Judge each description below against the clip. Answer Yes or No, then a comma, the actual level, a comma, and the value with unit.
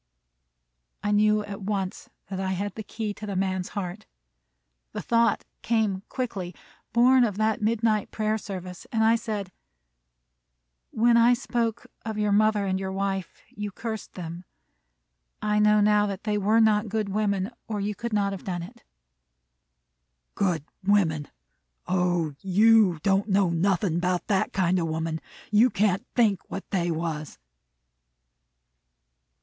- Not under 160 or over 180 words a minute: No, average, 145 wpm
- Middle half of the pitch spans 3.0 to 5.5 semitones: No, narrow, 2.5 semitones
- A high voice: Yes, high, 205 Hz